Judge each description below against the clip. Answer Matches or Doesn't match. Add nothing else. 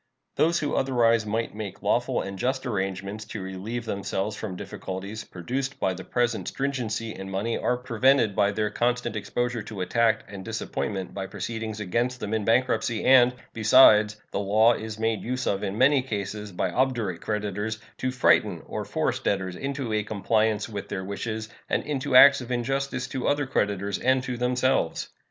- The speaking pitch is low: Matches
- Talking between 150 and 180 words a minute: Matches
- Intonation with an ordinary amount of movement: Matches